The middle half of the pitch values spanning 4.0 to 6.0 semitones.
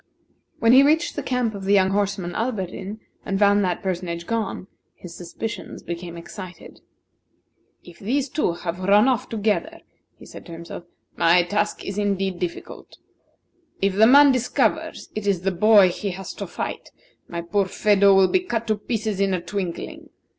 No: average, 3.4 semitones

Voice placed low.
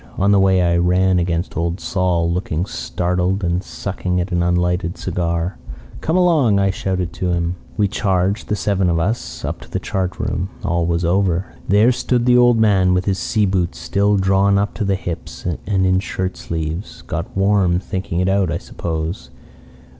Yes: very low, 95 Hz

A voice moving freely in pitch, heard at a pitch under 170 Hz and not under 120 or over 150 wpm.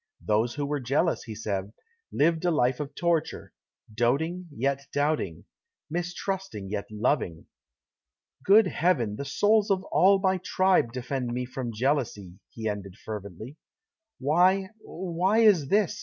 Yes: wide, 8.1 semitones; medium, 140 Hz; slow, 135 wpm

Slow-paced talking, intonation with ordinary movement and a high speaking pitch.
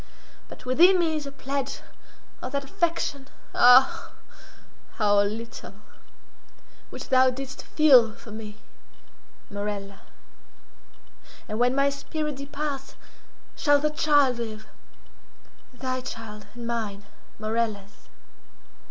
Yes: slow, 95 wpm; average, 4.5 semitones; very high, 255 Hz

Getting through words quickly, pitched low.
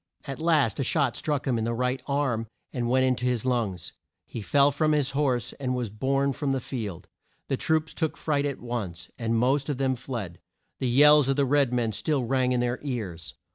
Yes: fast, 215 wpm; low, 130 Hz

